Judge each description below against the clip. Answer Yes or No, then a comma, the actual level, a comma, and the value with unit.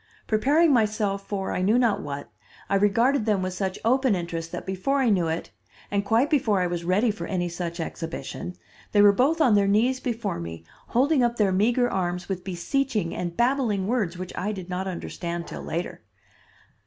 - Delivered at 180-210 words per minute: Yes, average, 190 wpm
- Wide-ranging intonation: No, average, 5.0 semitones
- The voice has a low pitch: No, high, 200 Hz